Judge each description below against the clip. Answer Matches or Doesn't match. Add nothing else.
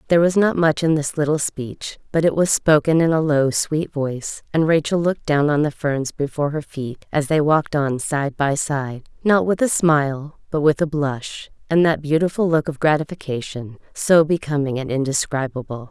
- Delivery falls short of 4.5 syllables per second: Doesn't match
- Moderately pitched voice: Matches